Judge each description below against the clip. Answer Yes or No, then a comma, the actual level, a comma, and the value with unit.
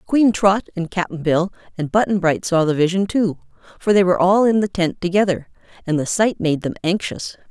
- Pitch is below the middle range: No, medium, 185 Hz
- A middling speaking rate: No, fast, 210 wpm